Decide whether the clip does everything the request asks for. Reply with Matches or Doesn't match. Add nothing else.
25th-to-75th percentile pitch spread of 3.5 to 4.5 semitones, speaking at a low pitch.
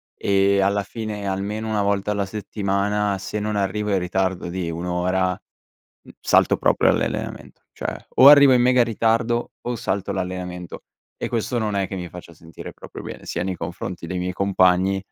Doesn't match